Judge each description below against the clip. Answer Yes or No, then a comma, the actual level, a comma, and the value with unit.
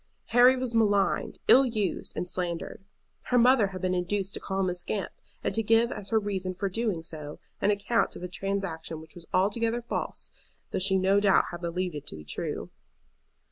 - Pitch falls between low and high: No, high, 195 Hz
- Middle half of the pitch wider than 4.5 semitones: No, average, 3.8 semitones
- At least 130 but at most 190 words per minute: No, average, 200 wpm